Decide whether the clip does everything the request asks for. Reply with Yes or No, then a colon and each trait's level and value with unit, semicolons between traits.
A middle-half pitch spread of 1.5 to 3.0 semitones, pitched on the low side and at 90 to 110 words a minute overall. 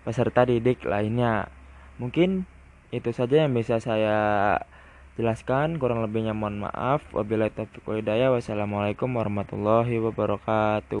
Yes: narrow, 2.6 semitones; low, 110 Hz; average, 100 wpm